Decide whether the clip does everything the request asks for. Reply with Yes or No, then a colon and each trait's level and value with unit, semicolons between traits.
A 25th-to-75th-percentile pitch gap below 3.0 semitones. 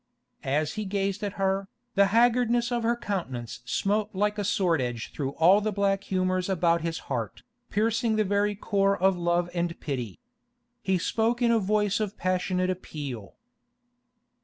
No: average, 3.5 semitones